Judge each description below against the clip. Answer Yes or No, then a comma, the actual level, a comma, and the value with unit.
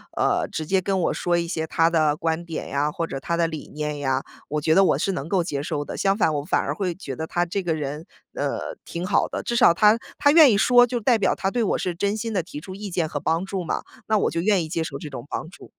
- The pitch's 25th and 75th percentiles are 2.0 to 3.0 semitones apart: No, average, 4.1 semitones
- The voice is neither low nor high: Yes, medium, 170 Hz